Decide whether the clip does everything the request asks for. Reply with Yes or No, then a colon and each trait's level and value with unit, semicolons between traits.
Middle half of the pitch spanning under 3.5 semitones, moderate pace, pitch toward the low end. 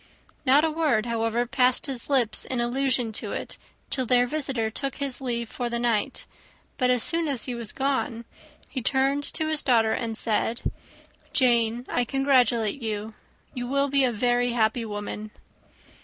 No: average, 3.0 semitones; average, 170 wpm; high, 245 Hz